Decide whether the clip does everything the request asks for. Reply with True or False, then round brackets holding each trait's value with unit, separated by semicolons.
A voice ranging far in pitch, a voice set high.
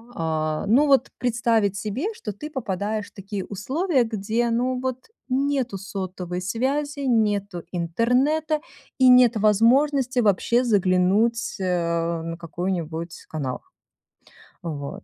True (5.8 semitones; 215 Hz)